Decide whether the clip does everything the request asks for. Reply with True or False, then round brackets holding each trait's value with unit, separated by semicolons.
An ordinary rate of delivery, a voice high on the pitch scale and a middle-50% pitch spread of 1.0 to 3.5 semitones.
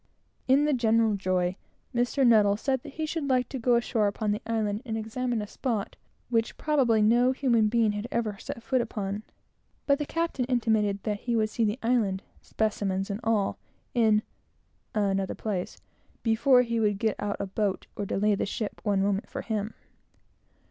True (175 wpm; 220 Hz; 2.9 semitones)